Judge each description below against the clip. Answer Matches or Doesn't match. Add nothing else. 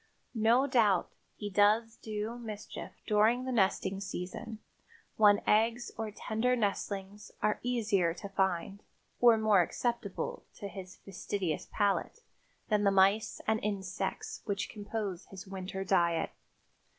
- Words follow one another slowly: Matches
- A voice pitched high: Matches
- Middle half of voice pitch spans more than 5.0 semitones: Doesn't match